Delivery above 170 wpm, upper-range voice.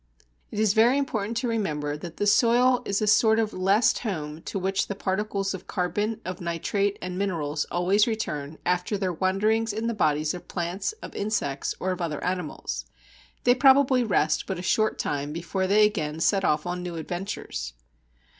Yes: average, 185 wpm; high, 195 Hz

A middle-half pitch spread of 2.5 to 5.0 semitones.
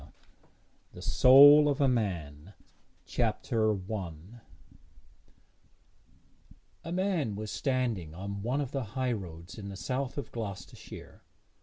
No: wide, 5.6 semitones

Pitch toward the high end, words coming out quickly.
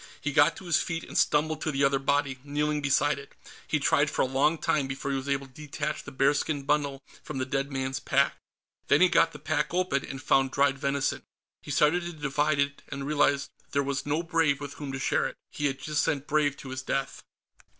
No: medium, 140 Hz; fast, 235 wpm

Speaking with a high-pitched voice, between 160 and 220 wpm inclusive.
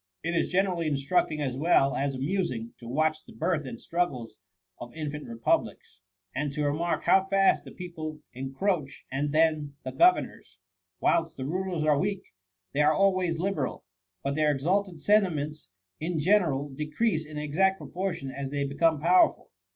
No: medium, 155 Hz; average, 165 wpm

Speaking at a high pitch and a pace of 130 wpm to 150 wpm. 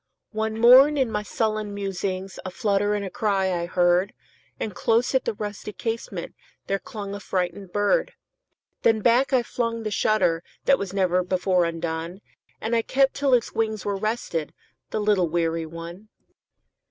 Yes: high, 205 Hz; average, 140 wpm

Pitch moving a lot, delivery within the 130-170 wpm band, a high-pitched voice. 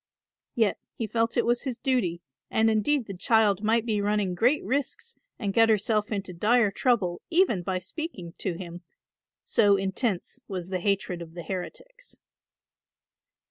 No: average, 4.2 semitones; average, 155 wpm; high, 210 Hz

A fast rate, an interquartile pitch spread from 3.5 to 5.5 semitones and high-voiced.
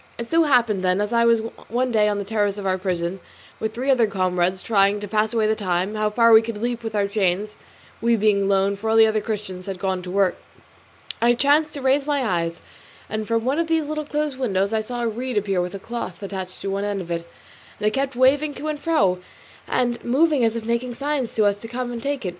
Yes: fast, 255 wpm; average, 3.9 semitones; high, 220 Hz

